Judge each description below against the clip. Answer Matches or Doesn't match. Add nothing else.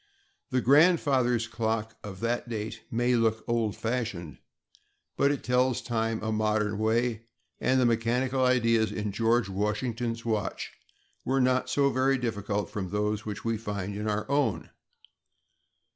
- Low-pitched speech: Matches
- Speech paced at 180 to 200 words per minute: Doesn't match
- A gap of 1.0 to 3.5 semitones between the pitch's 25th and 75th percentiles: Matches